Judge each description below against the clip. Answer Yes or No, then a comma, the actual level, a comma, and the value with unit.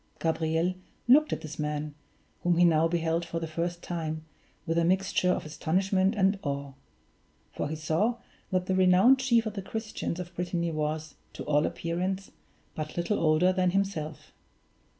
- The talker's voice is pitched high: No, medium, 170 Hz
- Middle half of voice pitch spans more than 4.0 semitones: No, average, 3.1 semitones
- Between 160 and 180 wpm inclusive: Yes, average, 165 wpm